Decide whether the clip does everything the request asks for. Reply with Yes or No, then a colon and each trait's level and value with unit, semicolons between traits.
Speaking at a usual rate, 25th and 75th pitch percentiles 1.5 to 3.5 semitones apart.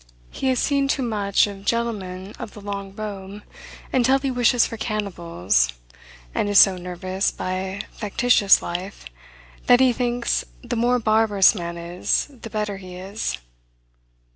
No: average, 145 wpm; average, 3.9 semitones